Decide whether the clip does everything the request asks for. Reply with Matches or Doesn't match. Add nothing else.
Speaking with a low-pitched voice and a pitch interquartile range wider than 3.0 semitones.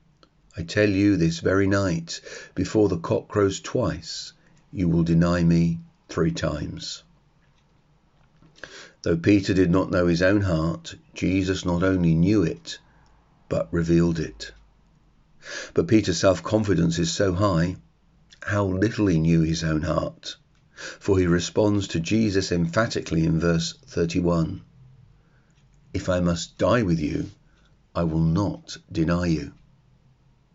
Matches